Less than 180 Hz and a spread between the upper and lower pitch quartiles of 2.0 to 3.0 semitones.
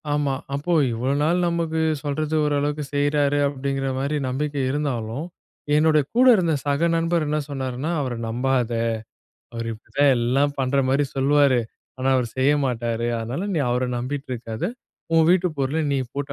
Yes: medium, 140 Hz; average, 2.7 semitones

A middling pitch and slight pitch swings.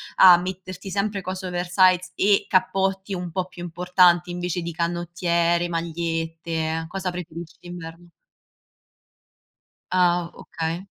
Yes: medium, 175 Hz; narrow, 1.6 semitones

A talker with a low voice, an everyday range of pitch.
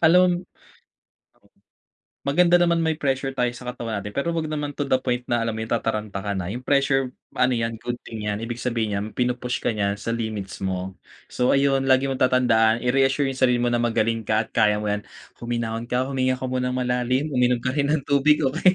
Yes: low, 125 Hz; average, 3.1 semitones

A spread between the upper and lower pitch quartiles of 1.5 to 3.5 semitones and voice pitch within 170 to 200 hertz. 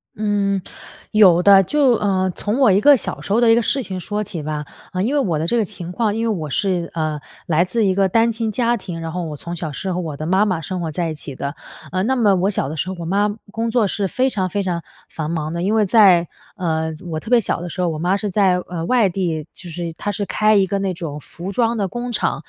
No: average, 4.0 semitones; high, 190 Hz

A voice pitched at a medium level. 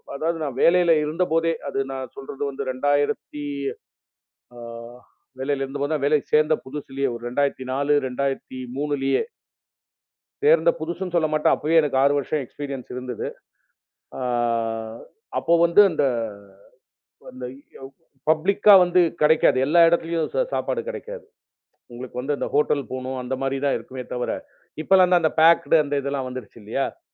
Yes: medium, 145 Hz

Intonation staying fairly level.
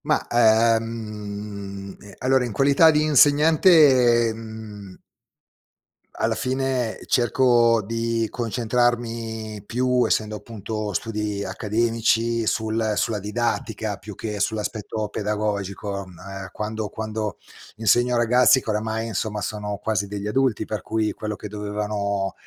Yes: narrow, 2.2 semitones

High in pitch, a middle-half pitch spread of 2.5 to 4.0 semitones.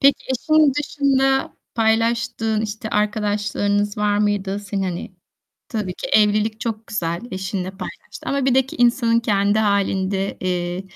Yes: high, 210 Hz; average, 2.8 semitones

